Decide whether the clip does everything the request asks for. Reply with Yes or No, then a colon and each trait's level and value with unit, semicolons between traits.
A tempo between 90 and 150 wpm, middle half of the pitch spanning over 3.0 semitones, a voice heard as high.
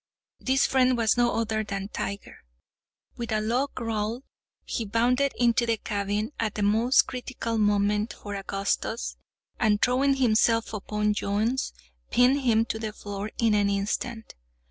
No: average, 145 wpm; average, 2.7 semitones; high, 220 Hz